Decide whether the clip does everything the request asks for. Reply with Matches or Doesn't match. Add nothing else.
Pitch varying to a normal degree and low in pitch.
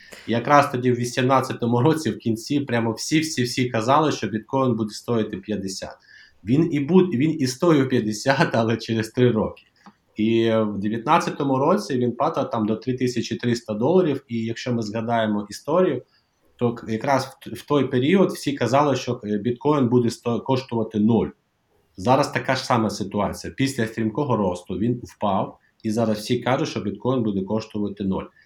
Matches